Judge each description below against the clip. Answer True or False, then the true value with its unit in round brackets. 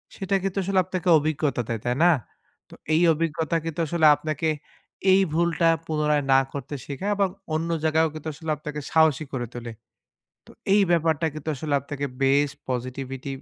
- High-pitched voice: False (155 Hz)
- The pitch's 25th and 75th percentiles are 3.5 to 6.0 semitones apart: False (2.8 semitones)